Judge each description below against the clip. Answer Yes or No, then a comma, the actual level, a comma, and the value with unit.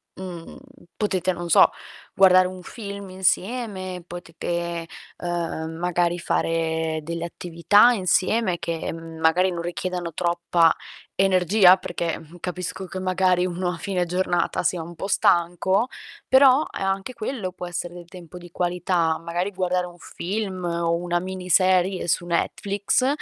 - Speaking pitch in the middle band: Yes, medium, 180 Hz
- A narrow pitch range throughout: Yes, narrow, 1.7 semitones